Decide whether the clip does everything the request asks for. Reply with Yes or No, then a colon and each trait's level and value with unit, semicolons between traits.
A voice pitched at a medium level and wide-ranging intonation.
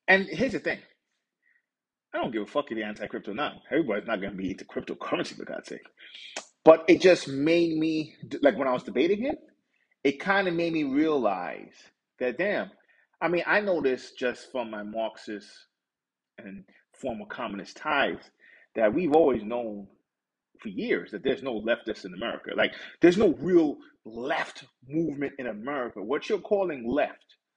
Yes: medium, 155 Hz; wide, 7.1 semitones